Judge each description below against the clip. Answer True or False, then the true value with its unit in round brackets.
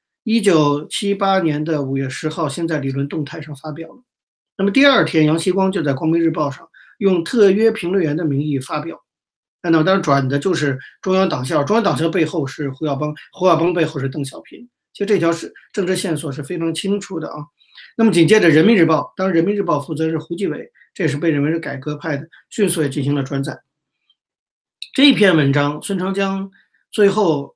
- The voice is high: False (165 Hz)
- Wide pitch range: False (4.5 semitones)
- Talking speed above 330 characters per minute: False (305 characters per minute)